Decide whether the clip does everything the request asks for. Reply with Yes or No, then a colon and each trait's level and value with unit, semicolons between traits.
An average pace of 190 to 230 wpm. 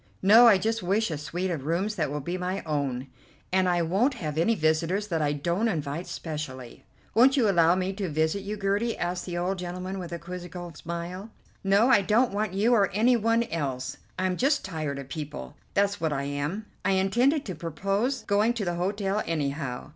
Yes: average, 200 wpm